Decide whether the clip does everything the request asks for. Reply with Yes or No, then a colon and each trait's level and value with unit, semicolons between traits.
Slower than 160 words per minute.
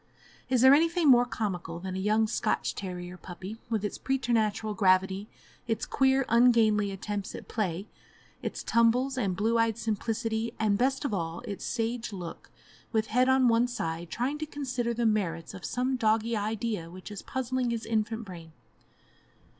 No: average, 165 wpm